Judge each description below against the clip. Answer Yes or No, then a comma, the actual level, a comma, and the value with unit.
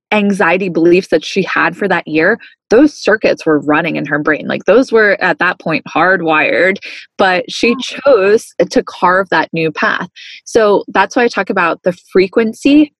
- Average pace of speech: Yes, average, 175 wpm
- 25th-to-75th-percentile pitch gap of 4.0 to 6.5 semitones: Yes, wide, 5.4 semitones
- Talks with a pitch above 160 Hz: Yes, high, 190 Hz